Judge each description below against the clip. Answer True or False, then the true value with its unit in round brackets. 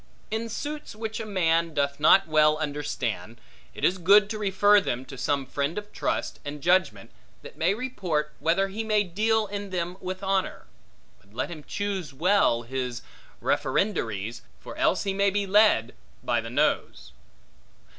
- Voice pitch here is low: False (180 Hz)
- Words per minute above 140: True (165 wpm)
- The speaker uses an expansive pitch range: True (6.2 semitones)